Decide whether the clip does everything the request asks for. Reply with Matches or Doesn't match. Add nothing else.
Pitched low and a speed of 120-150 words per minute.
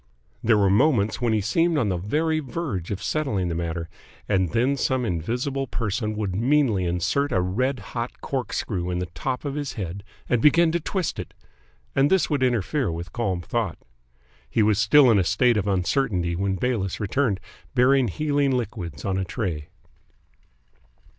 Doesn't match